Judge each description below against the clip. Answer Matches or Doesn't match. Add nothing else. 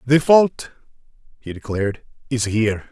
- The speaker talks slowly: Matches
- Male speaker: Matches